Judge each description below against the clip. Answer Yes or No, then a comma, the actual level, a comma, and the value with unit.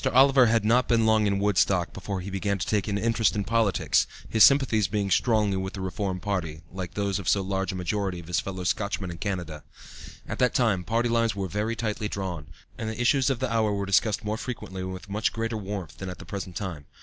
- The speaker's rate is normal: No, fast, 235 wpm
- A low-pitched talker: Yes, low, 100 Hz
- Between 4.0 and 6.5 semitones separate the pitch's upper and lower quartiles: No, average, 2.9 semitones